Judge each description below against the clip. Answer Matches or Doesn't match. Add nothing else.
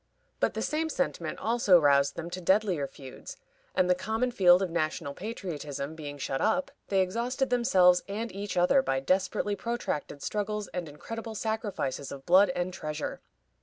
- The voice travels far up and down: Matches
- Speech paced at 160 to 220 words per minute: Matches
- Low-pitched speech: Doesn't match